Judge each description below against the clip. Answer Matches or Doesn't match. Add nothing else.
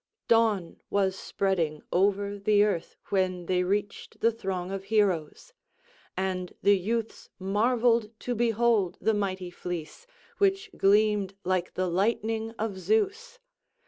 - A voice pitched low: Doesn't match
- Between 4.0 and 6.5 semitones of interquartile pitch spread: Doesn't match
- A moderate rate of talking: Doesn't match